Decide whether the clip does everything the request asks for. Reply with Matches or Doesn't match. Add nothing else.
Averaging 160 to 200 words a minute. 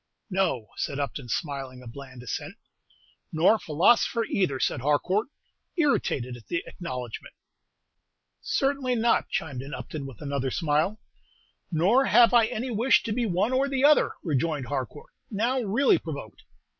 Doesn't match